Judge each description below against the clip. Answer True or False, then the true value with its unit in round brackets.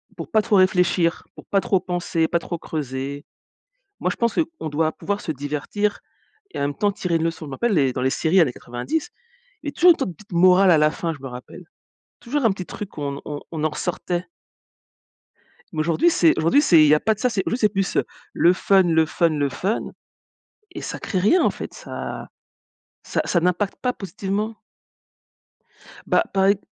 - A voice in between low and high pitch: True (175 Hz)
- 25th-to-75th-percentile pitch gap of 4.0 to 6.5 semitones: True (4.6 semitones)